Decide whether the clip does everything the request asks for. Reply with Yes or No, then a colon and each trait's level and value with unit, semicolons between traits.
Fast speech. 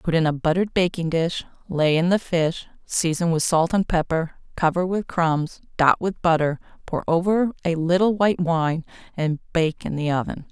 No: average, 185 wpm